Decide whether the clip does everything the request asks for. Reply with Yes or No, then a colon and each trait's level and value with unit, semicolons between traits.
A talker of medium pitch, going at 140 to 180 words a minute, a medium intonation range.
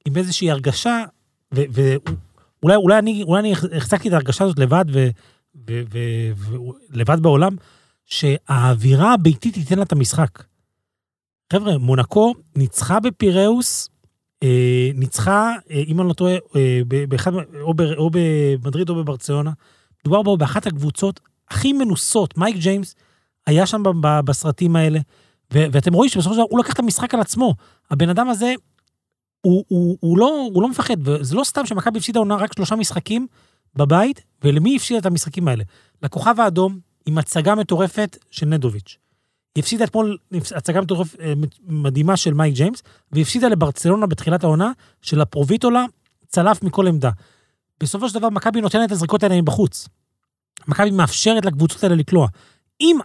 No: medium, 170 Hz; average, 145 wpm; wide, 6.3 semitones